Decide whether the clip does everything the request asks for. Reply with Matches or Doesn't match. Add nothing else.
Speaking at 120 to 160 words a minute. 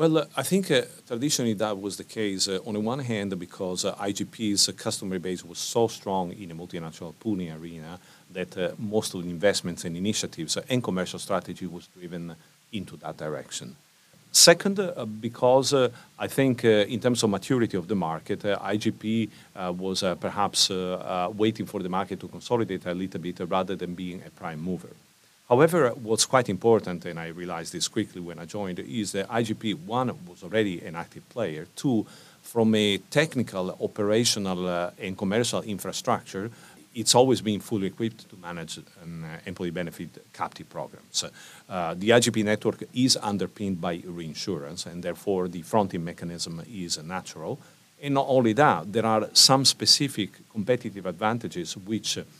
Doesn't match